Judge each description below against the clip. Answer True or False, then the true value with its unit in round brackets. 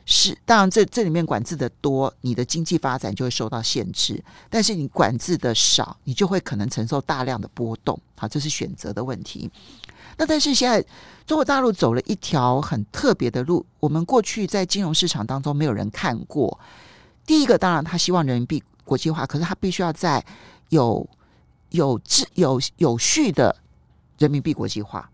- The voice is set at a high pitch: False (150 Hz)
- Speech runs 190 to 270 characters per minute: False (290 characters per minute)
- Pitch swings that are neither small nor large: False (6.6 semitones)